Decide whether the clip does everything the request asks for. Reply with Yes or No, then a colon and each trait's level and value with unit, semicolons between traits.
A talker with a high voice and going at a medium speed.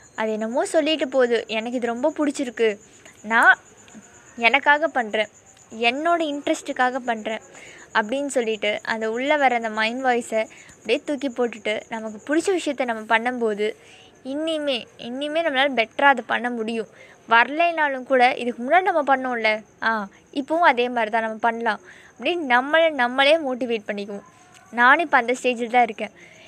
No: high, 245 Hz; fast, 140 wpm